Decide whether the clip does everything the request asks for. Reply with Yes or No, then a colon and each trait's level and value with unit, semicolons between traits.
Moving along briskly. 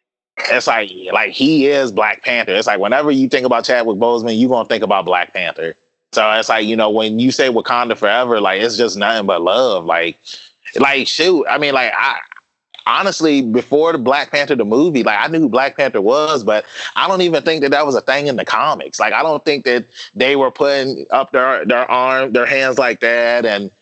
Yes: fast, 225 wpm